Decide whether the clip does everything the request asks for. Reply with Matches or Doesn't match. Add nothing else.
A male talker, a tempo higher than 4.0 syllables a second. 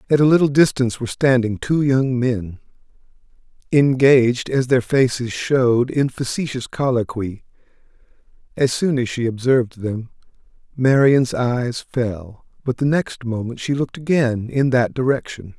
Matches